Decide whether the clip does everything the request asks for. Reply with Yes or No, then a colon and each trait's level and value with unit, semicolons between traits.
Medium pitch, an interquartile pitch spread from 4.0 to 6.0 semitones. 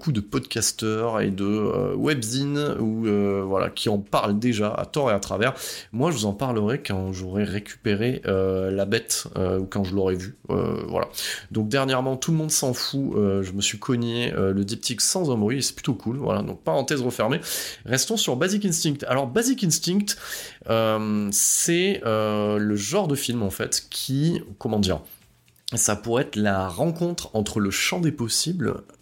No: low, 110 Hz; average, 5.2 semitones